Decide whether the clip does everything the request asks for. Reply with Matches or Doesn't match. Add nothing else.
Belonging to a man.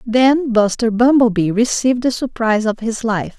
Doesn't match